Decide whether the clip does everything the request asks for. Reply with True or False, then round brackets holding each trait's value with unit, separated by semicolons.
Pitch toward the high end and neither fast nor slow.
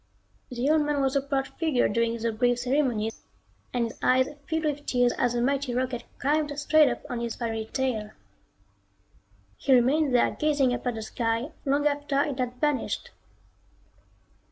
True (260 Hz; 170 wpm)